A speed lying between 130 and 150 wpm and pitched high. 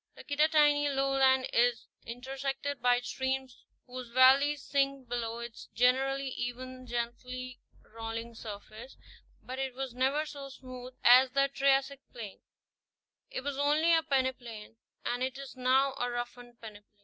Yes: average, 140 wpm; very high, 260 Hz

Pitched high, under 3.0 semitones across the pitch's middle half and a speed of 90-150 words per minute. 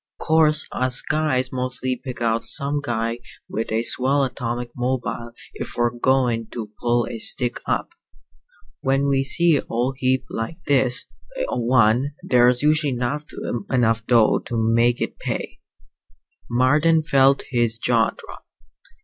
No: low, 125 Hz; narrow, 2.5 semitones; average, 140 wpm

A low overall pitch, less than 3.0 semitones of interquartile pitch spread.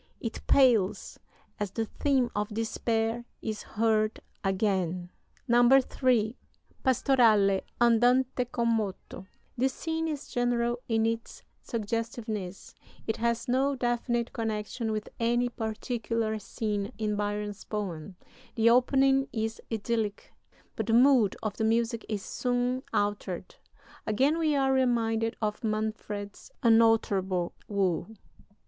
No: high, 225 Hz; narrow, 2.5 semitones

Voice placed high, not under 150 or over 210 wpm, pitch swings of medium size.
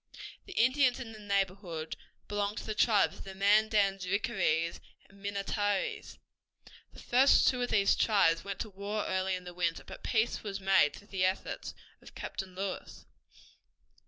No: high, 200 Hz; average, 160 wpm; narrow, 2.3 semitones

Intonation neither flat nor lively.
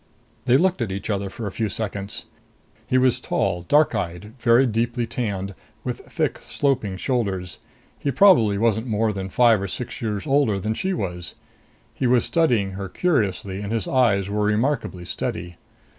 Yes: average, 4.2 semitones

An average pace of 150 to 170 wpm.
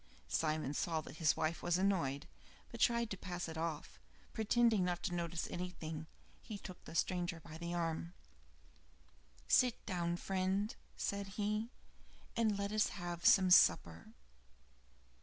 No: average, 140 wpm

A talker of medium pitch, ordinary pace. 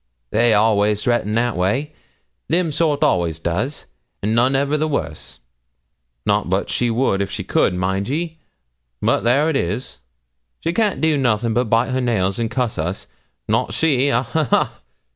No: low, 120 Hz; average, 170 wpm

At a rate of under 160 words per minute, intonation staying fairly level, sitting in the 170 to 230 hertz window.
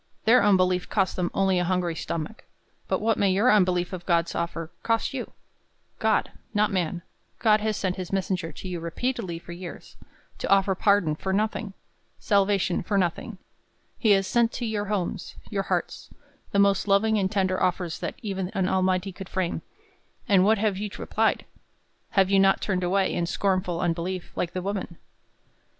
No: average, 175 wpm; narrow, 2.3 semitones; high, 190 Hz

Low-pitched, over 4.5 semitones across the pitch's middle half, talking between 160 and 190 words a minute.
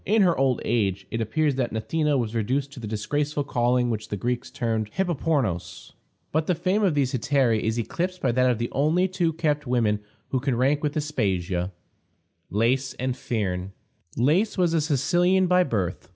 Yes: low, 130 Hz; wide, 5.6 semitones; average, 180 wpm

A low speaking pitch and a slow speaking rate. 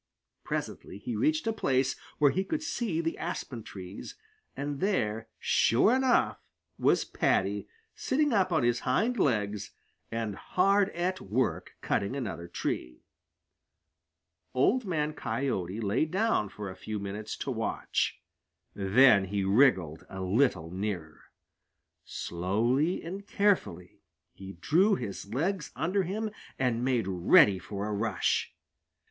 Yes: low, 125 Hz; slow, 130 wpm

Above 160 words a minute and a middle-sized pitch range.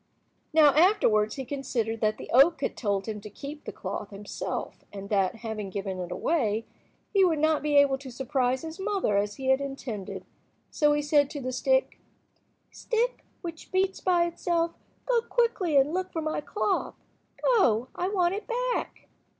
No: average, 175 wpm; wide, 7.9 semitones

